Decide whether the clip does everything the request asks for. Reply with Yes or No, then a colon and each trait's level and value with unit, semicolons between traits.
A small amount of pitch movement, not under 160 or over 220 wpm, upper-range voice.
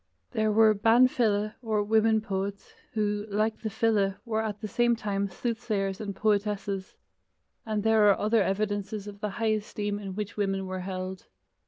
Yes: narrow, 1.7 semitones; average, 170 wpm; high, 210 Hz